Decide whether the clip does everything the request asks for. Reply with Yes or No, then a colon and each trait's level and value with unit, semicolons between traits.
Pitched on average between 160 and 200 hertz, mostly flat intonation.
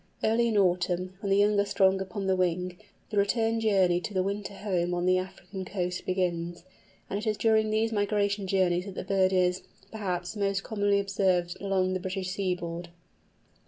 Yes: high, 190 Hz; narrow, 2.0 semitones